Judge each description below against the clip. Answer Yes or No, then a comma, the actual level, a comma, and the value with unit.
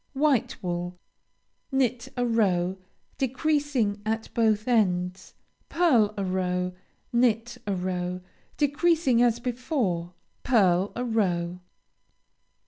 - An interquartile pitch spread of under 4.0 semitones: No, wide, 5.5 semitones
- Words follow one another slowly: Yes, slow, 100 wpm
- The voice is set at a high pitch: Yes, high, 220 Hz